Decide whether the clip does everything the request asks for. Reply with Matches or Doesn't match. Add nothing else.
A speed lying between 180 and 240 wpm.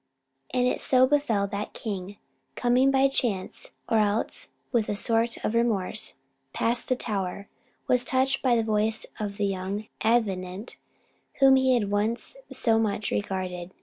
Doesn't match